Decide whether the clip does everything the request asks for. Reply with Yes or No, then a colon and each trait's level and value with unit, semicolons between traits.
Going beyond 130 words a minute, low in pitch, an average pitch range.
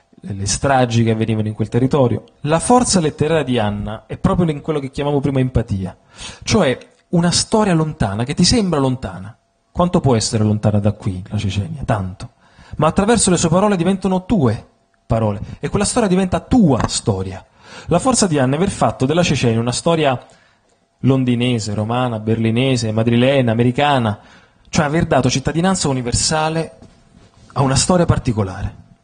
No: average, 155 wpm; low, 130 Hz; wide, 6.6 semitones